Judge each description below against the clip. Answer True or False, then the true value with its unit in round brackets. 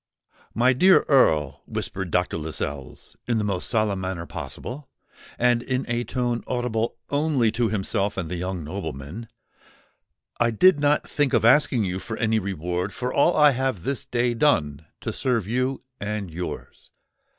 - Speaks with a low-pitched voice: True (115 Hz)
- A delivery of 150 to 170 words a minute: True (160 wpm)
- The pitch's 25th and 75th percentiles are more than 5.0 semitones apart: True (5.6 semitones)